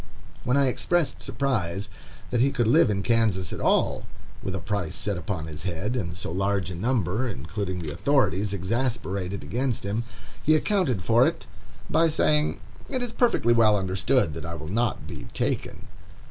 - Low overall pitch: Yes, low, 105 Hz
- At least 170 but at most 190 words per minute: Yes, average, 175 wpm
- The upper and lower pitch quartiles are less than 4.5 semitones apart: No, wide, 5.6 semitones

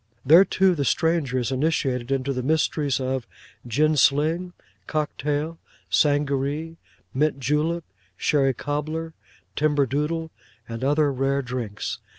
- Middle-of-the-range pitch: Yes, medium, 145 Hz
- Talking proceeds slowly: Yes, slow, 125 wpm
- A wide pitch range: No, average, 2.9 semitones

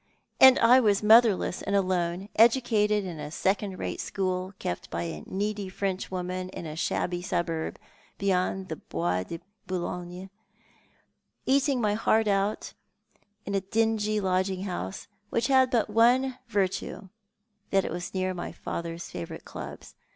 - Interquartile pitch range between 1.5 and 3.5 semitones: Yes, average, 3.2 semitones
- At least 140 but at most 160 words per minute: Yes, average, 150 wpm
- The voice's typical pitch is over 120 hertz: Yes, high, 190 Hz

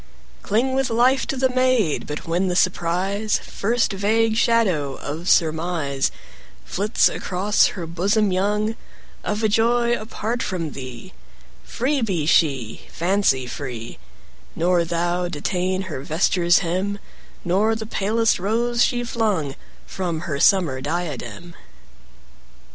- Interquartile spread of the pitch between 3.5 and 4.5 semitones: No, average, 5.1 semitones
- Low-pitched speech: No, medium, 185 Hz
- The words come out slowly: Yes, slow, 130 wpm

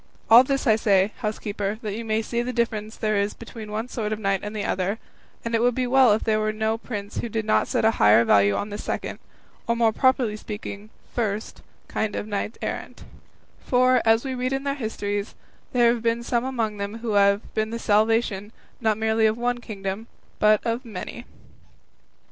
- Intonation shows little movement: Yes, narrow, 2.2 semitones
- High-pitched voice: Yes, high, 220 Hz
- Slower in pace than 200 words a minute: No, fast, 205 wpm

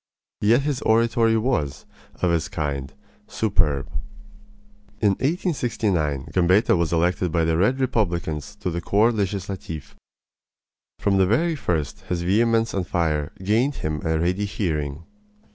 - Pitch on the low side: Yes, very low, 90 Hz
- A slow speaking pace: Yes, slow, 130 wpm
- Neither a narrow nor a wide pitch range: No, wide, 5.7 semitones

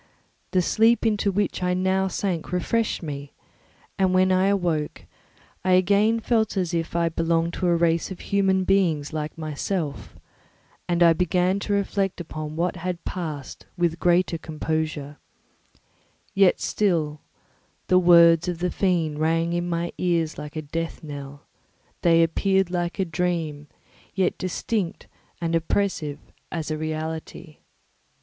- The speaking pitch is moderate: Yes, medium, 170 Hz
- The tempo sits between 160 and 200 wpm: No, average, 140 wpm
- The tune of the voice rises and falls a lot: No, average, 2.8 semitones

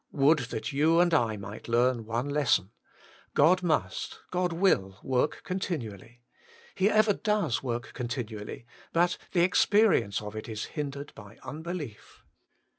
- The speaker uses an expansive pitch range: Yes, wide, 7.3 semitones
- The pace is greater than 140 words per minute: No, slow, 135 wpm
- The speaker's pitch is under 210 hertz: Yes, medium, 140 Hz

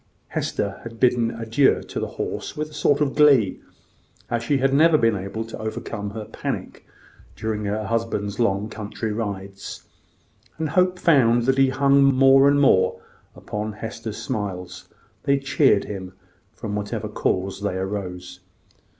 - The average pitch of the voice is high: No, low, 115 Hz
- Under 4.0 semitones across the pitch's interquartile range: No, average, 4.9 semitones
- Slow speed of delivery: No, average, 150 wpm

